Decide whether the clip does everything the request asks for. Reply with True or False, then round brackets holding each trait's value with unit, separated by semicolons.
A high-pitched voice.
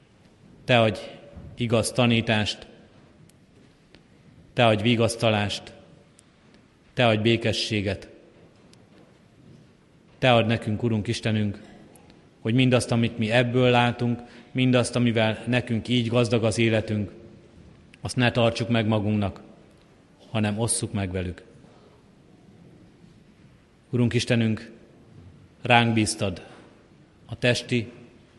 False (115 Hz)